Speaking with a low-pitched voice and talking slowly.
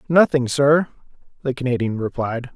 Yes: low, 130 Hz; slow, 115 wpm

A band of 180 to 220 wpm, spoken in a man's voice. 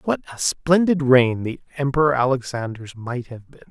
No: average, 160 wpm; male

